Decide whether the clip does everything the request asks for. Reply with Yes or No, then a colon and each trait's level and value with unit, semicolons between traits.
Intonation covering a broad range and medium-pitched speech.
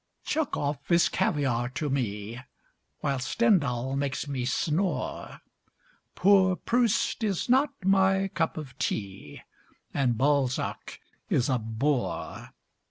Yes: wide, 7.2 semitones; medium, 145 Hz